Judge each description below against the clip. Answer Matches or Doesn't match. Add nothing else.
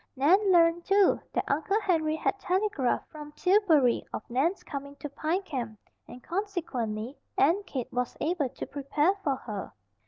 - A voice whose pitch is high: Matches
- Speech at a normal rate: Matches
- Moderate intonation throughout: Doesn't match